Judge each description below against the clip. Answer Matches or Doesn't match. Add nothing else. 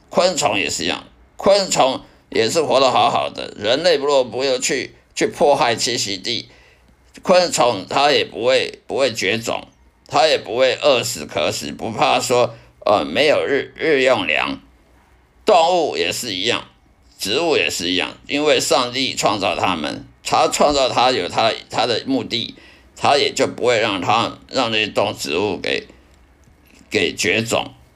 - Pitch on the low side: Matches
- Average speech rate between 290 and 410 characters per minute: Doesn't match